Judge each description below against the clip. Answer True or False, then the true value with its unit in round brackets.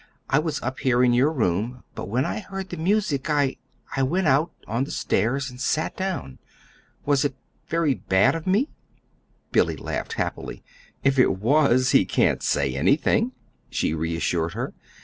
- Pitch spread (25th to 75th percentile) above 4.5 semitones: True (5.0 semitones)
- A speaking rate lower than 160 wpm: False (170 wpm)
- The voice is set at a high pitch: False (135 Hz)